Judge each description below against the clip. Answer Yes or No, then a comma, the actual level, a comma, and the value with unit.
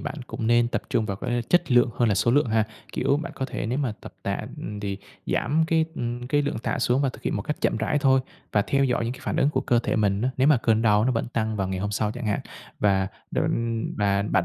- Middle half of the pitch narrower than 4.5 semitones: Yes, average, 4.0 semitones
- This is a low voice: Yes, low, 120 Hz